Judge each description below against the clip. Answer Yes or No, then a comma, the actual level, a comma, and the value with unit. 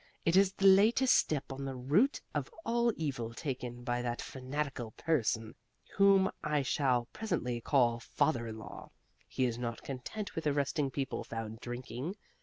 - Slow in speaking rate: No, average, 160 wpm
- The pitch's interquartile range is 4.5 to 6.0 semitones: Yes, average, 5.1 semitones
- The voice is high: No, low, 135 Hz